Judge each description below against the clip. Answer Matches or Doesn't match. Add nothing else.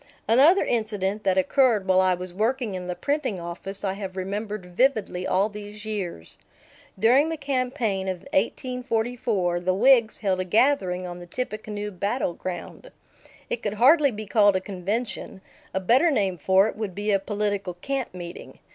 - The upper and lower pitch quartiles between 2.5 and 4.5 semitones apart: Matches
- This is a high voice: Matches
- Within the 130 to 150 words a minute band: Doesn't match